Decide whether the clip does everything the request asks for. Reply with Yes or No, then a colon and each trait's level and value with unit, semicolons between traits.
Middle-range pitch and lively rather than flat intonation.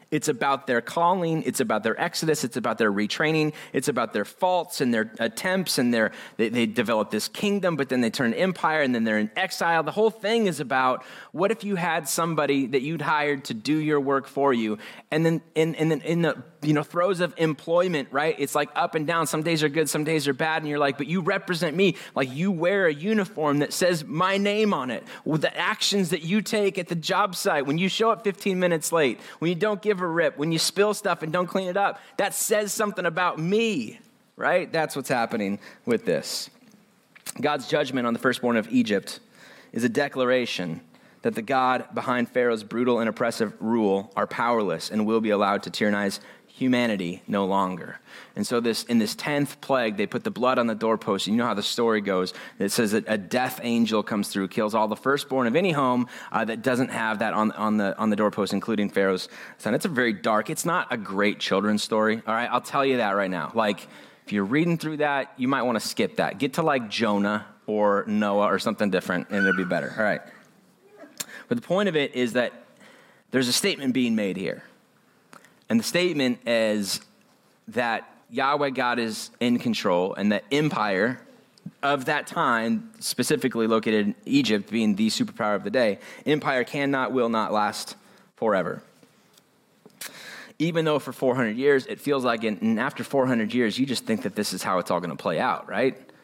Yes: medium, 145 Hz; wide, 7.5 semitones